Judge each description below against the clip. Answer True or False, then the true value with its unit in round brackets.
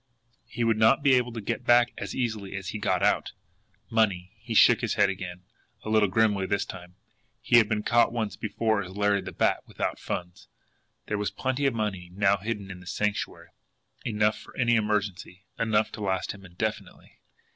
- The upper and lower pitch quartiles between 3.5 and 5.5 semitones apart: False (2.6 semitones)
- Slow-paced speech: False (190 wpm)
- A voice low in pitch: True (105 Hz)